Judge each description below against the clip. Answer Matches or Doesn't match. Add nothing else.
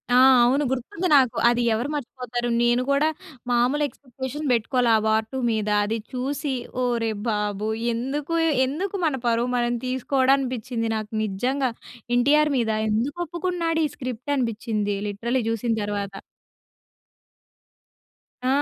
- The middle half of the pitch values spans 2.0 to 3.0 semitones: Doesn't match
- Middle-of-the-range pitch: Doesn't match